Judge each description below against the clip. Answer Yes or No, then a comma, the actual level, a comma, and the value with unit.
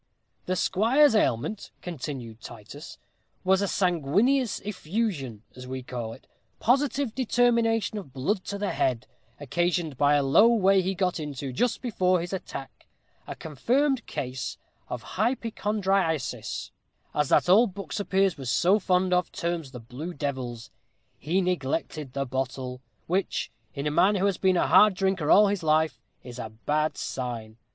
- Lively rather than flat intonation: Yes, wide, 6.9 semitones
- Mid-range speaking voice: Yes, medium, 175 Hz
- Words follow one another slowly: No, average, 155 wpm